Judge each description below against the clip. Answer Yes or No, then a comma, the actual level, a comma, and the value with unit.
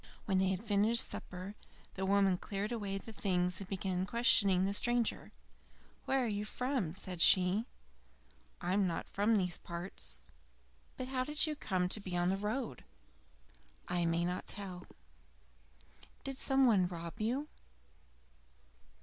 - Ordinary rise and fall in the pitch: Yes, average, 3.9 semitones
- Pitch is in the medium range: No, high, 195 Hz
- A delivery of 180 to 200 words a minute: No, average, 150 wpm